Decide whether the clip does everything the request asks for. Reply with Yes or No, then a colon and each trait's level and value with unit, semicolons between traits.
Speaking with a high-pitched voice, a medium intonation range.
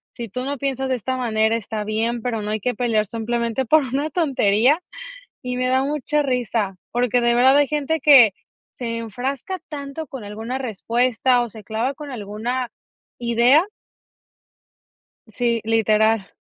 Yes: high, 245 Hz; average, 3.1 semitones